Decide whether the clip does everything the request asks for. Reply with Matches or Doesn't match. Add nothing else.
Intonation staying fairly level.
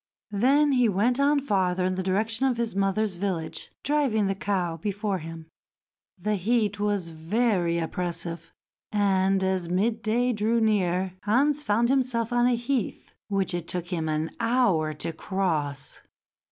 Doesn't match